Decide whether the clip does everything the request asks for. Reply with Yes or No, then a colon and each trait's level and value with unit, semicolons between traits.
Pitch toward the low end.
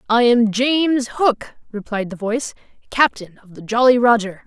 No: high, 230 Hz